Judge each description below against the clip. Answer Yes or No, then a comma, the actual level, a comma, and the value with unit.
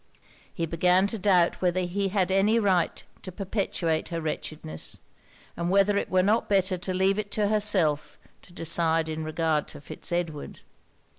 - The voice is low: No, medium, 180 Hz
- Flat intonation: No, average, 3.1 semitones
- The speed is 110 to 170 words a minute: Yes, average, 165 wpm